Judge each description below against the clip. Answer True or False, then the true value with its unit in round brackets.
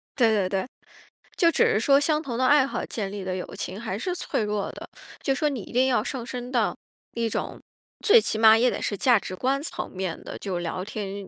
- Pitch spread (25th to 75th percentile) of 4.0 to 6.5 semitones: True (5.1 semitones)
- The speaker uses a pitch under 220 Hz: False (230 Hz)